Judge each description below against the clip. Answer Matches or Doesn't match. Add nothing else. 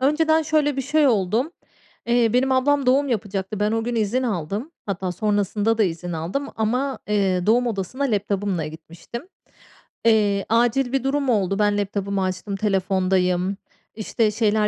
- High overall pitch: Matches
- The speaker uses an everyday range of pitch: Matches